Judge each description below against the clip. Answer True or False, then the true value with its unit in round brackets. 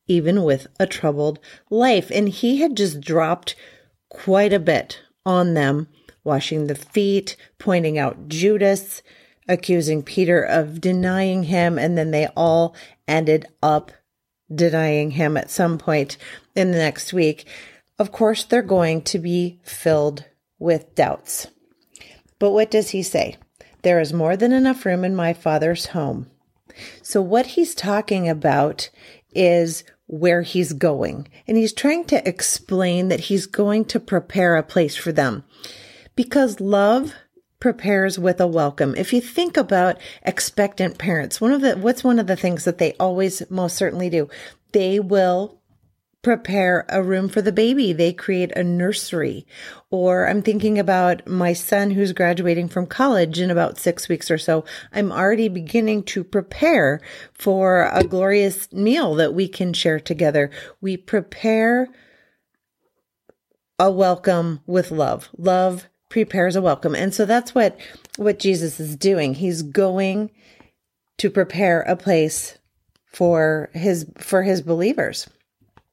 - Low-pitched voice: False (185 Hz)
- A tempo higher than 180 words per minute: False (145 wpm)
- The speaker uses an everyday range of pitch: True (3.4 semitones)